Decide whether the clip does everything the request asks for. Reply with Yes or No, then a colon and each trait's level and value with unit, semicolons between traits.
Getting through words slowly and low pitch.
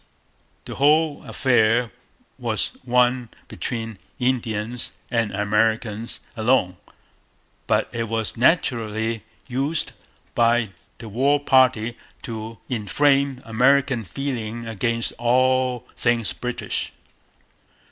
Yes: slow, 90 wpm; low, 120 Hz